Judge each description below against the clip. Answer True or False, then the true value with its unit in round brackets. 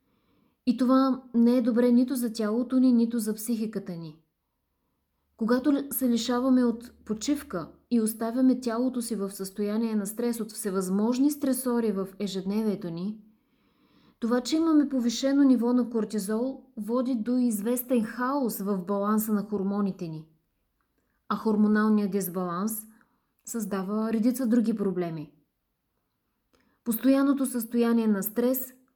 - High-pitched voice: True (230 Hz)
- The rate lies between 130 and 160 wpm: False (120 wpm)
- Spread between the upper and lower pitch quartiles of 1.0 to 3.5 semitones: True (3.2 semitones)